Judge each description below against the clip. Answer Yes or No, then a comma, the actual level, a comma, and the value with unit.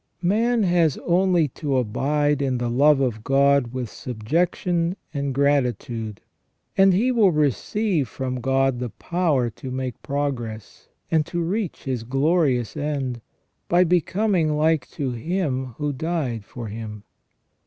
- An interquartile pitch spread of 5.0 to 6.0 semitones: Yes, average, 5.3 semitones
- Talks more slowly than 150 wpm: Yes, slow, 135 wpm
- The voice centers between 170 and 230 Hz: No, medium, 140 Hz